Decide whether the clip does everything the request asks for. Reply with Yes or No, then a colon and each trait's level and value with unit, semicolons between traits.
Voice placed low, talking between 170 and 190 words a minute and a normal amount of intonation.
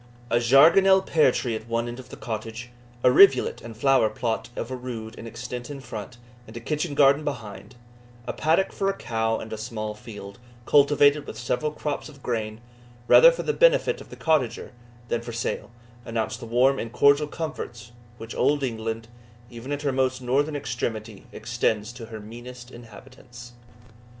Yes: low, 120 Hz; average, 180 wpm; average, 3.9 semitones